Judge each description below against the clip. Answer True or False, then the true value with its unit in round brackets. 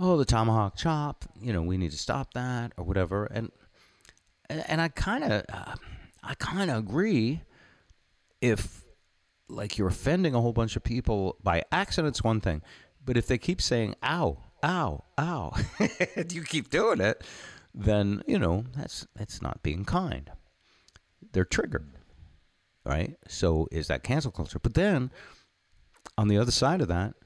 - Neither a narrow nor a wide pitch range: False (6.9 semitones)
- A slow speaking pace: False (165 wpm)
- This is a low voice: True (110 Hz)